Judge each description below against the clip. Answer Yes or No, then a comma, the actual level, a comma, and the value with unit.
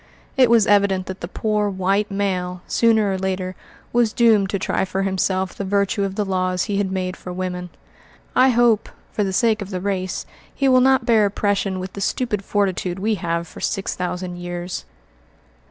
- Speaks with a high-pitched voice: Yes, high, 195 Hz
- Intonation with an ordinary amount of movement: No, narrow, 2.3 semitones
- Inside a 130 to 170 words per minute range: No, average, 190 wpm